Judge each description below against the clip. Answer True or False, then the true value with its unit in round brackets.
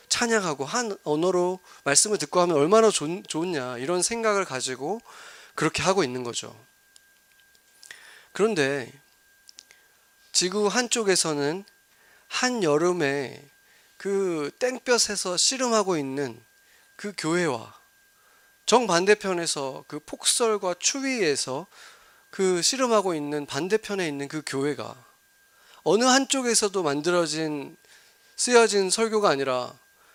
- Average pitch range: False (7.2 semitones)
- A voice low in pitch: False (190 Hz)